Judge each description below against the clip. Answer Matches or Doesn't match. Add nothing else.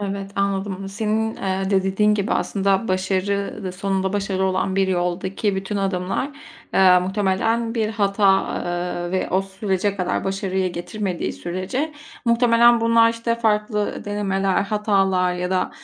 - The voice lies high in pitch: Matches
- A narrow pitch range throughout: Matches